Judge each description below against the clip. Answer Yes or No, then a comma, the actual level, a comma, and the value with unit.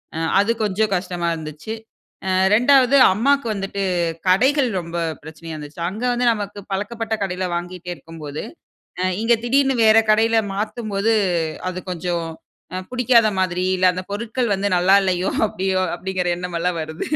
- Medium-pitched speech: No, high, 195 Hz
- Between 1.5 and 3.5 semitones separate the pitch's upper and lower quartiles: No, average, 4.2 semitones